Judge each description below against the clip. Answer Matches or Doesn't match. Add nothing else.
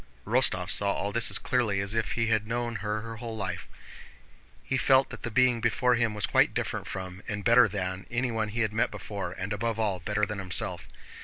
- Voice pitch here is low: Matches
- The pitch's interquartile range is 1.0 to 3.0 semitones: Matches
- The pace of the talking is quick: Matches